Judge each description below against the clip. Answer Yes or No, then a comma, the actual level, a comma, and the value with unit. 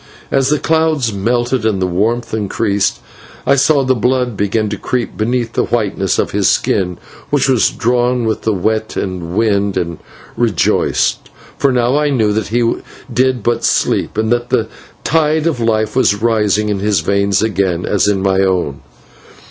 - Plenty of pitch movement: No, average, 3.8 semitones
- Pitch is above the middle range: No, low, 110 Hz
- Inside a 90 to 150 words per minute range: No, average, 170 wpm